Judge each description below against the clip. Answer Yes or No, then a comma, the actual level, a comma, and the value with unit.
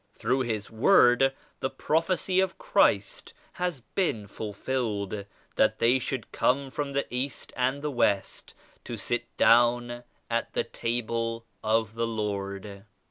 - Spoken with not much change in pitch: No, average, 3.7 semitones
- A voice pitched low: Yes, low, 120 Hz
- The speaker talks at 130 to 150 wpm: Yes, average, 140 wpm